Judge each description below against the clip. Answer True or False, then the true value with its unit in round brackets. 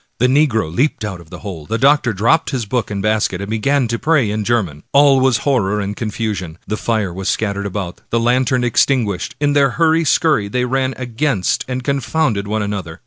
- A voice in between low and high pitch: False (115 Hz)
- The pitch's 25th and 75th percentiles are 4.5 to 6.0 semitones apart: True (4.8 semitones)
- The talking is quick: True (215 wpm)